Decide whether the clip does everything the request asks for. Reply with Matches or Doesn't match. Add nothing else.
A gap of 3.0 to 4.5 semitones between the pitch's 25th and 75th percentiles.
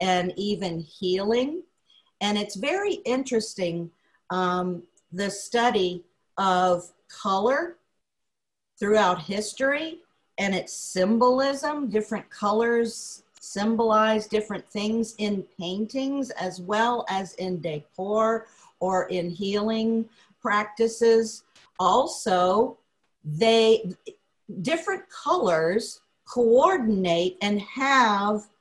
Matches